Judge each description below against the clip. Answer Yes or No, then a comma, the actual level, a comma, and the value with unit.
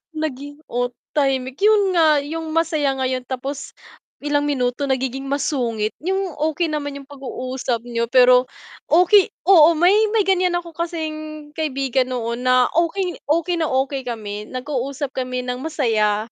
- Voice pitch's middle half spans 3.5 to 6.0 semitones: Yes, average, 4.0 semitones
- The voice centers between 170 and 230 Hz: No, very high, 280 Hz